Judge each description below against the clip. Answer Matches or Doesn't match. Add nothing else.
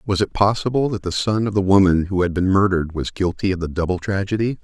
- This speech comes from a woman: Doesn't match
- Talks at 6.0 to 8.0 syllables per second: Matches